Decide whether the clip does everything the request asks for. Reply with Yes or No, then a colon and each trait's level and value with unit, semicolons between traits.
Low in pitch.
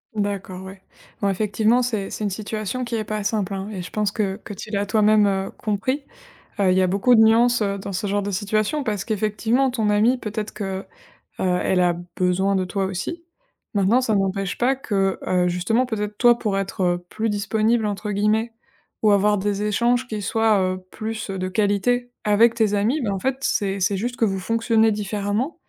No: high, 210 Hz